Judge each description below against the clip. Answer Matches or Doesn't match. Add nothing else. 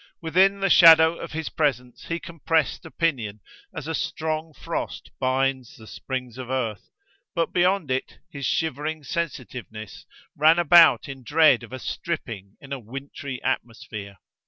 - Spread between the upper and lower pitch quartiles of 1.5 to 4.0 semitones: Doesn't match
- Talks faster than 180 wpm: Doesn't match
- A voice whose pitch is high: Doesn't match